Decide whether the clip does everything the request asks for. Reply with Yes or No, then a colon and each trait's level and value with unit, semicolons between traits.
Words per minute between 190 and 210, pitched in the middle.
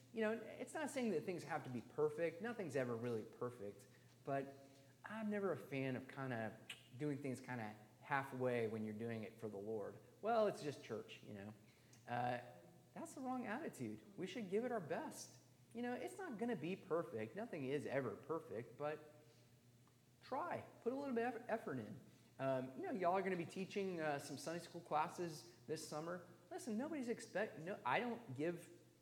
Yes: average, 200 wpm; medium, 150 Hz